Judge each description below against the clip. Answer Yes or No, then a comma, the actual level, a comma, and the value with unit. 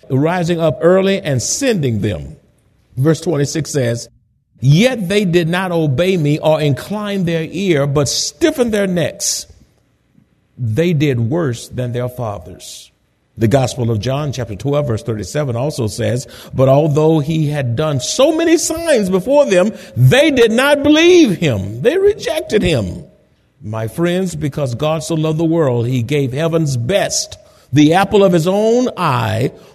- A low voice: No, medium, 155 Hz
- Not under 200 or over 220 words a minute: No, average, 150 wpm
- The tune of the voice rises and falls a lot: Yes, wide, 7.1 semitones